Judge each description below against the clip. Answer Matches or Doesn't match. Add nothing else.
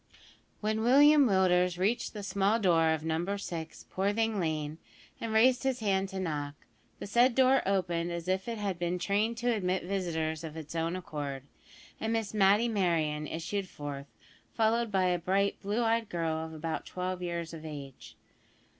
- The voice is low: Doesn't match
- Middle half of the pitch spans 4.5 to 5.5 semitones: Matches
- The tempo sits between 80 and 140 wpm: Doesn't match